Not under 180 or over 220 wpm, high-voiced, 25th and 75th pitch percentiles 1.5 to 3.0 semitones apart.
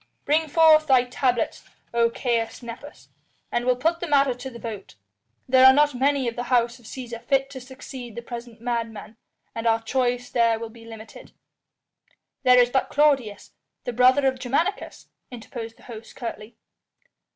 No: average, 170 wpm; high, 245 Hz; narrow, 2.4 semitones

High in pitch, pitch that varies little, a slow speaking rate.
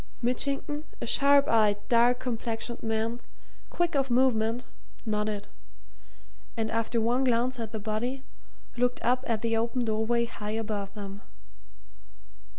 Yes: high, 230 Hz; narrow, 2.2 semitones; slow, 130 wpm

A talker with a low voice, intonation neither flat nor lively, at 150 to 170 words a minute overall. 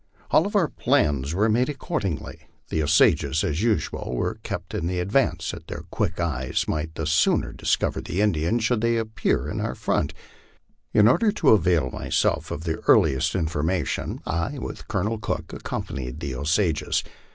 No: very low, 85 Hz; wide, 6.1 semitones; average, 165 wpm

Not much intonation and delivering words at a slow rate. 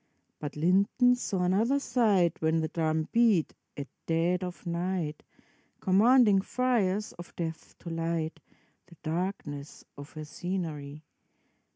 No: average, 3.9 semitones; slow, 125 wpm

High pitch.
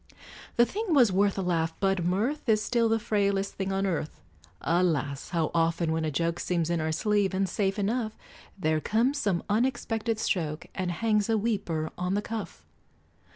Yes: high, 195 Hz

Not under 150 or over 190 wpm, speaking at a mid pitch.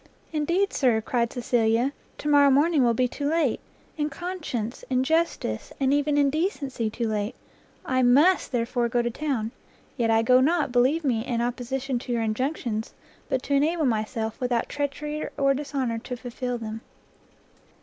No: average, 165 wpm; very high, 255 Hz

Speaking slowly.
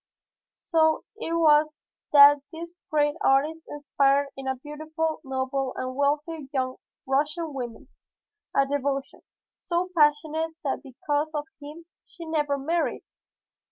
Yes: slow, 125 wpm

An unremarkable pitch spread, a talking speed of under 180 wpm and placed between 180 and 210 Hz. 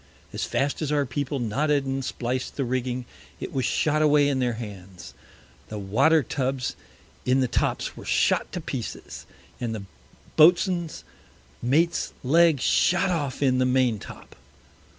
No: average, 3.4 semitones; average, 150 wpm; low, 135 Hz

